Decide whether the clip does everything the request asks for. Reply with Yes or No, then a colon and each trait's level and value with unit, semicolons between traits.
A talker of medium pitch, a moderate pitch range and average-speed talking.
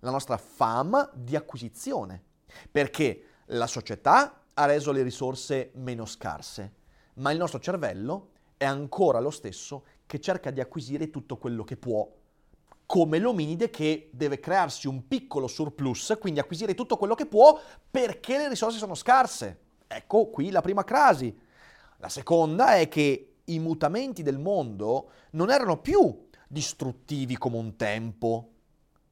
No: medium, 145 Hz; wide, 5.7 semitones; average, 140 wpm